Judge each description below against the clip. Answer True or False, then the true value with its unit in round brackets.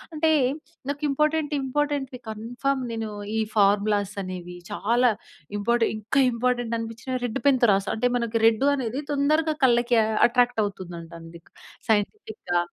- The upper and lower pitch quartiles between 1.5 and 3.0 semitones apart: False (4.5 semitones)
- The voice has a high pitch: True (235 Hz)